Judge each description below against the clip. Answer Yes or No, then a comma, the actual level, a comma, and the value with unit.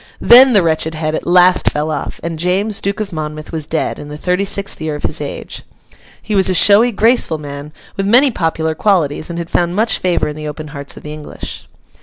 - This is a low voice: No, medium, 170 Hz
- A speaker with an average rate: No, fast, 225 wpm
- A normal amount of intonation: Yes, average, 4.5 semitones